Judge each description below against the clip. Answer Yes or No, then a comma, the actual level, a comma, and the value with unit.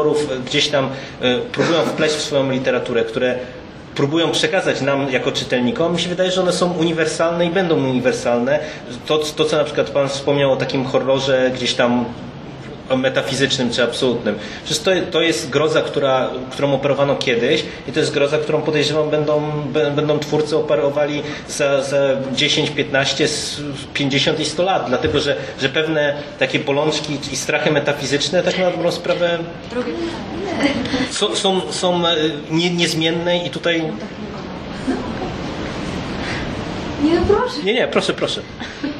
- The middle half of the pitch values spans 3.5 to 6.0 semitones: No, average, 3.1 semitones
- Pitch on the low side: No, medium, 150 Hz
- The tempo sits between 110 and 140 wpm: Yes, average, 130 wpm